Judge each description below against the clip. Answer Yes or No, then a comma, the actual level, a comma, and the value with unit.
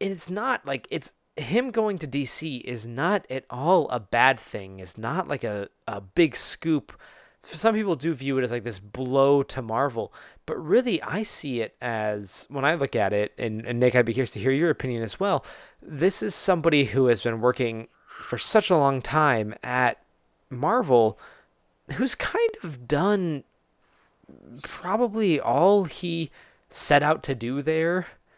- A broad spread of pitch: Yes, wide, 6.1 semitones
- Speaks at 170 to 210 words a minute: Yes, average, 175 wpm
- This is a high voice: No, medium, 140 Hz